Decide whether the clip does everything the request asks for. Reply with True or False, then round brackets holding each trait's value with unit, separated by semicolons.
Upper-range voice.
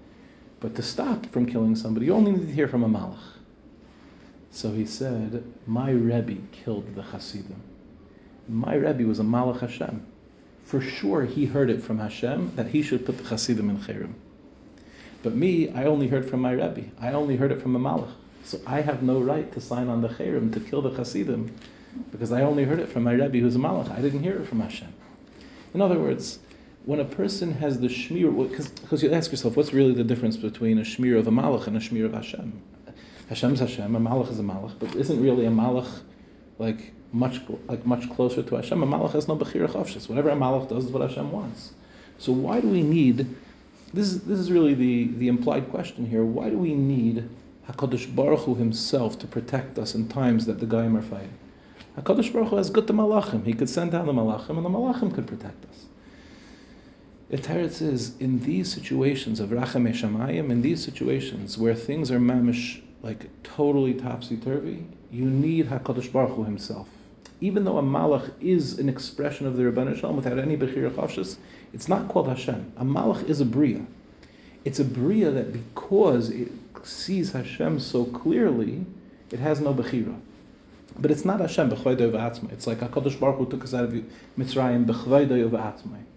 False (125 Hz)